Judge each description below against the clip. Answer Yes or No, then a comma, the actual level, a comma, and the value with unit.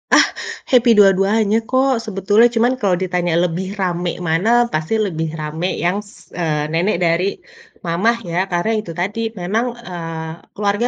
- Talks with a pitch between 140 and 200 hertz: Yes, medium, 185 Hz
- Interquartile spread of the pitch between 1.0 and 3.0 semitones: No, average, 3.9 semitones